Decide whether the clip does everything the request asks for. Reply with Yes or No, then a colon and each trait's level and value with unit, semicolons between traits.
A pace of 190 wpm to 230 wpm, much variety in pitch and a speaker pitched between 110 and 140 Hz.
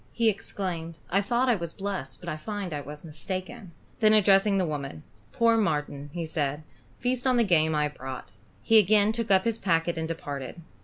No: average, 200 wpm; wide, 5.8 semitones; medium, 185 Hz